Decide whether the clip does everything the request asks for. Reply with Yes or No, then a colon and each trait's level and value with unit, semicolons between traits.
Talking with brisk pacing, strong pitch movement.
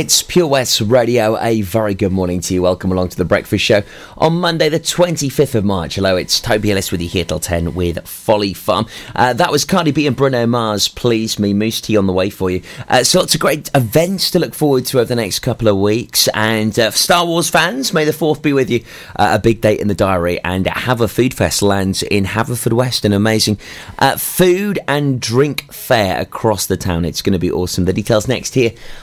Yes: fast, 230 wpm; wide, 6.2 semitones